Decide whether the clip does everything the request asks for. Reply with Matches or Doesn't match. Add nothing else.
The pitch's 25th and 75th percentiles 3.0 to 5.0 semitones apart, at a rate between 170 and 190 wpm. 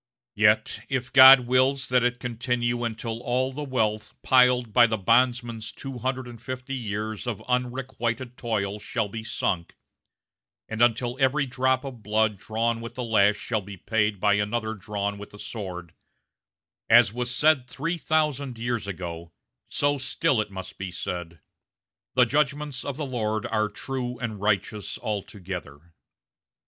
Doesn't match